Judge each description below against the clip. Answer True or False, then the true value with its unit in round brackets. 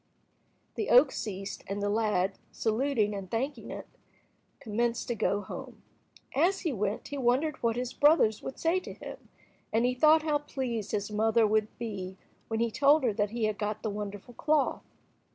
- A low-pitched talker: False (230 Hz)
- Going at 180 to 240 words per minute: True (185 wpm)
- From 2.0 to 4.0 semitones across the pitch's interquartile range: False (4.4 semitones)